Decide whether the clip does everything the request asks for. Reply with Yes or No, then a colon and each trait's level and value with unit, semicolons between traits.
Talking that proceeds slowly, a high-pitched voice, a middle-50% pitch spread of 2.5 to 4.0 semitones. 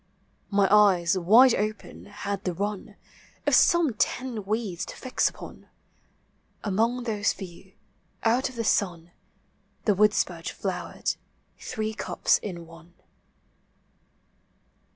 Yes: slow, 110 wpm; high, 205 Hz; average, 3.6 semitones